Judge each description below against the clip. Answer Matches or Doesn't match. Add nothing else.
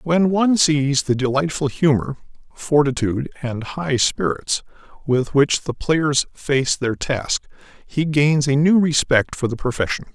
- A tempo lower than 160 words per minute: Matches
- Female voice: Doesn't match